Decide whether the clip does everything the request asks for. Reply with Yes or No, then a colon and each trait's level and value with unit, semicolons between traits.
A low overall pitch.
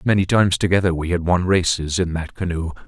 Yes: very low, 90 Hz